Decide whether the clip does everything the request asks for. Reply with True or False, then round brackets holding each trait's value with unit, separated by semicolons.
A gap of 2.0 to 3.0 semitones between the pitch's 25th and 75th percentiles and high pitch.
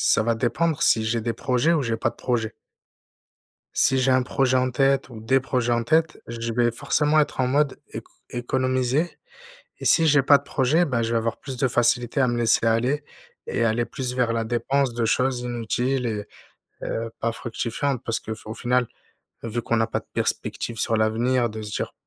False (2.5 semitones; 120 Hz)